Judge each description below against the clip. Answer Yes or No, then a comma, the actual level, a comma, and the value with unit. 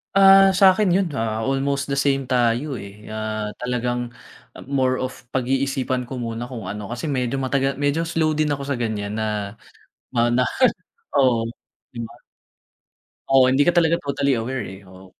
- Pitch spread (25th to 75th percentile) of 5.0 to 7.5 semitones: No, average, 3.4 semitones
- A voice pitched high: No, low, 130 Hz